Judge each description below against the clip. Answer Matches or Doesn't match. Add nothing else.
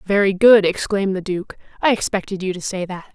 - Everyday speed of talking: Doesn't match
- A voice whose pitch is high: Matches